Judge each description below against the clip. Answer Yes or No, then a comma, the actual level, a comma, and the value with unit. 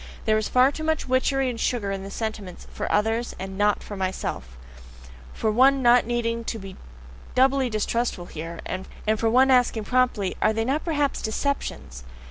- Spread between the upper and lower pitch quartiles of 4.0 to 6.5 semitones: Yes, average, 4.3 semitones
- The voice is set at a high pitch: Yes, high, 230 Hz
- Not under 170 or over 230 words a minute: Yes, average, 175 wpm